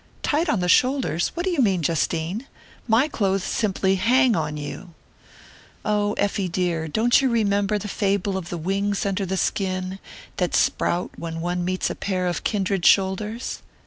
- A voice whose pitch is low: No, high, 195 Hz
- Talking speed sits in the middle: Yes, average, 170 wpm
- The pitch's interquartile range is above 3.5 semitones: No, average, 3.0 semitones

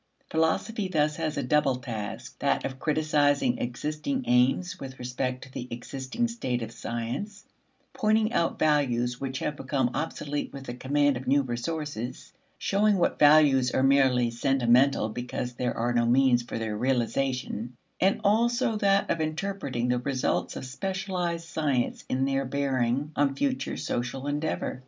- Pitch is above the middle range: No, low, 135 Hz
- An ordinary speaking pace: Yes, average, 150 wpm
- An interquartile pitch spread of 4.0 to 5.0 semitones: Yes, average, 4.4 semitones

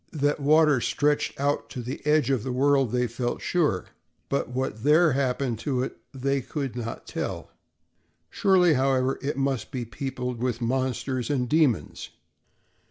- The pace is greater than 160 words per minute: No, average, 155 wpm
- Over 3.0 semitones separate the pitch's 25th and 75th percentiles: No, narrow, 2.5 semitones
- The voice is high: No, low, 130 Hz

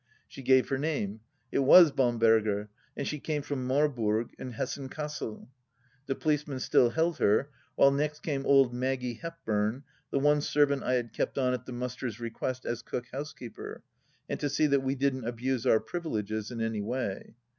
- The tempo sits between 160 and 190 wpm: Yes, average, 180 wpm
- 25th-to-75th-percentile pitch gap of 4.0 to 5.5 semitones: No, average, 3.4 semitones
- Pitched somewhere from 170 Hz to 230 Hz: No, low, 130 Hz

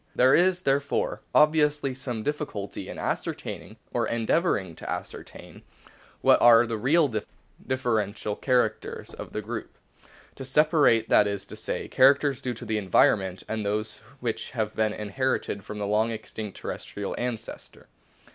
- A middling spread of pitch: Yes, average, 4.2 semitones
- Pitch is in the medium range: No, low, 115 Hz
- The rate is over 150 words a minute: No, average, 145 wpm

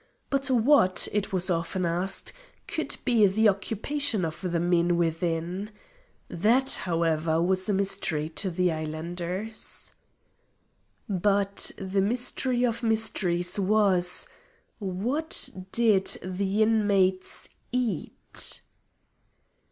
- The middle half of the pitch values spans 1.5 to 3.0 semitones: No, average, 3.8 semitones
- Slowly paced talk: Yes, slow, 100 wpm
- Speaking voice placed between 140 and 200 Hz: Yes, high, 190 Hz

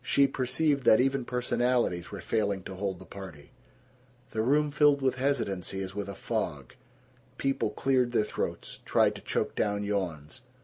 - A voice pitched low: Yes, low, 115 Hz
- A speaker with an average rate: Yes, average, 165 wpm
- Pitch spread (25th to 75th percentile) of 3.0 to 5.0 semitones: No, wide, 5.5 semitones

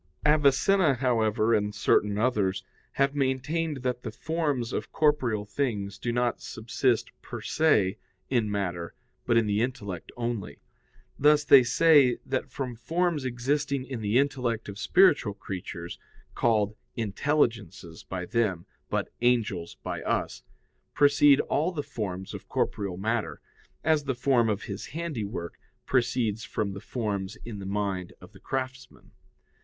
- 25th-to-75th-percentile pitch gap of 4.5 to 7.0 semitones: Yes, average, 5.2 semitones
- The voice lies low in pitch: Yes, low, 120 Hz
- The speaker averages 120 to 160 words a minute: Yes, average, 140 wpm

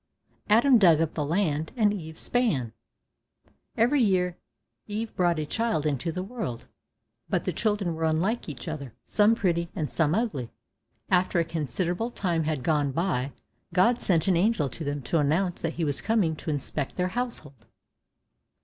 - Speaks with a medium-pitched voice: Yes, medium, 170 Hz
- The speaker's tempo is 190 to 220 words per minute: No, average, 165 wpm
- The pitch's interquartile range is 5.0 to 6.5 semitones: Yes, wide, 5.4 semitones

